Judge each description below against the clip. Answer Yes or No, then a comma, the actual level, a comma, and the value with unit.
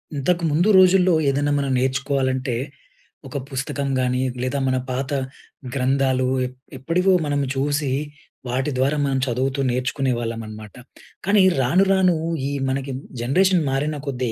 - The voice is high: No, low, 135 Hz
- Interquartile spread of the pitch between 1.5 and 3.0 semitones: Yes, narrow, 2.5 semitones